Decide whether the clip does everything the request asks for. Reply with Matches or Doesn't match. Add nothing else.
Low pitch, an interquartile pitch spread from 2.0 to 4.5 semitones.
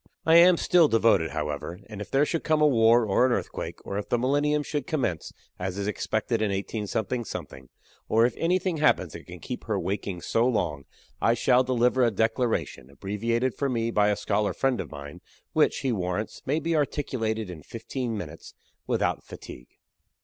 Doesn't match